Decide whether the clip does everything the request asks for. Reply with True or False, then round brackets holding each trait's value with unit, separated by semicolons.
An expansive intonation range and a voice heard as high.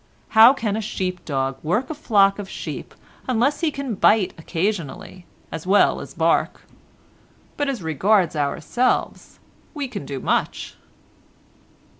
True (7.1 semitones; 205 Hz)